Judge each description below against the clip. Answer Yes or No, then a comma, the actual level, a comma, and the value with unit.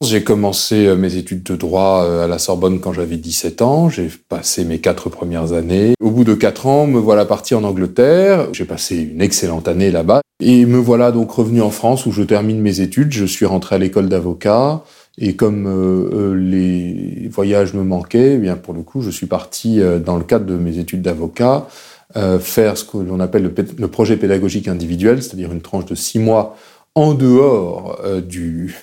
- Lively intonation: No, average, 3.7 semitones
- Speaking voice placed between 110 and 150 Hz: No, low, 100 Hz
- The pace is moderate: Yes, average, 190 wpm